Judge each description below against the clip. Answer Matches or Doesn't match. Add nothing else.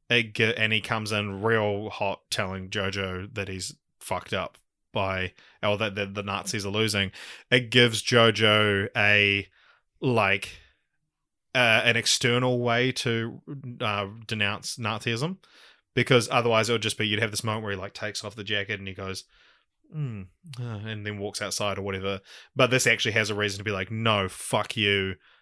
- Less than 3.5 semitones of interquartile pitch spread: Matches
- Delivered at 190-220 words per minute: Doesn't match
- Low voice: Matches